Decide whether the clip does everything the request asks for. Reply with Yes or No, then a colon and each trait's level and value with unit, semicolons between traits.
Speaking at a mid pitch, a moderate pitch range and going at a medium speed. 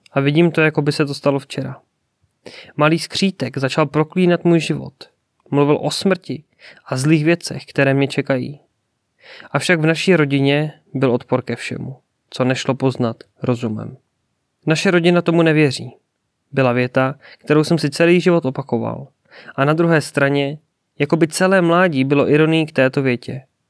Yes: medium, 145 Hz; average, 3.5 semitones; average, 155 wpm